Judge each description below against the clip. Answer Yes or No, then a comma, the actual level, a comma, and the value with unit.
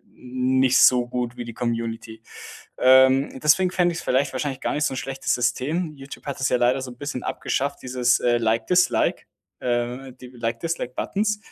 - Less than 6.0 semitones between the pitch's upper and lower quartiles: Yes, narrow, 2.4 semitones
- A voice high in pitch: No, low, 130 Hz